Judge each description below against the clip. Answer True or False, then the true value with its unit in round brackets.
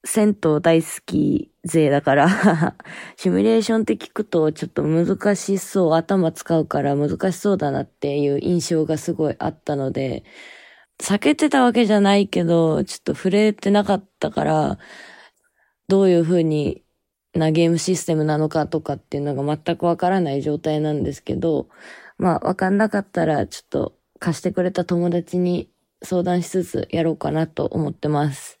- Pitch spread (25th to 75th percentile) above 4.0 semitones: False (3.7 semitones)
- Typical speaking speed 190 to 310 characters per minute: False (340 characters per minute)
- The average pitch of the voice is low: False (170 Hz)